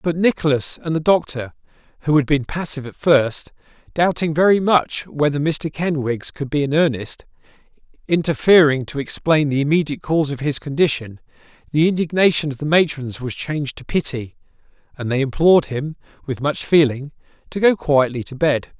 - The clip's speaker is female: No, male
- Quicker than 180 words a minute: No, average, 155 wpm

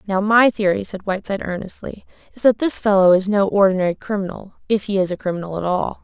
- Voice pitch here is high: Yes, high, 195 Hz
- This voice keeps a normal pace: No, fast, 210 wpm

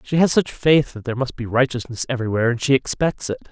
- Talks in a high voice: No, low, 130 Hz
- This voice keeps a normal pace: No, fast, 240 wpm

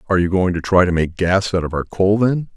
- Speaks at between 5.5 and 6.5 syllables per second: Yes, 6.0 syllables/s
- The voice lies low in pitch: Yes, very low, 95 Hz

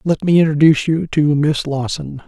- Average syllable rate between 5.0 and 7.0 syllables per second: Yes, 5.1 syllables/s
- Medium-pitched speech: Yes, medium, 150 Hz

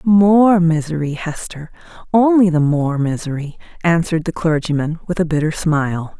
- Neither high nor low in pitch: Yes, medium, 165 Hz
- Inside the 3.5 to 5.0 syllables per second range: Yes, 4.9 syllables/s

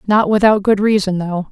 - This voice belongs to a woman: Yes, female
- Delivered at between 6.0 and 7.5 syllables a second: No, 5.2 syllables/s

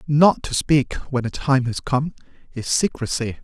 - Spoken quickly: No, average, 175 wpm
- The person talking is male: Yes, male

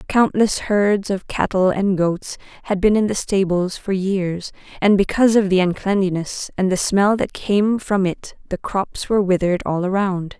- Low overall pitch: No, high, 195 Hz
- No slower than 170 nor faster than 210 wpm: Yes, average, 180 wpm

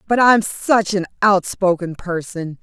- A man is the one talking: No, female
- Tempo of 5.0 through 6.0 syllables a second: No, 3.9 syllables/s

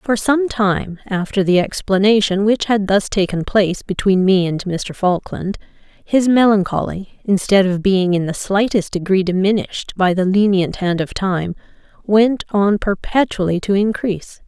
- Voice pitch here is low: No, high, 195 Hz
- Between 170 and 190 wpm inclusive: No, average, 155 wpm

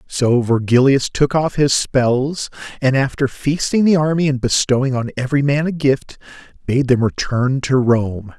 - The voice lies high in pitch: No, low, 135 Hz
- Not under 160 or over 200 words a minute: Yes, average, 165 wpm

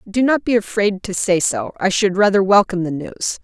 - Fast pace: Yes, fast, 225 wpm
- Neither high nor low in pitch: No, high, 195 Hz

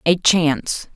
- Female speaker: Yes, female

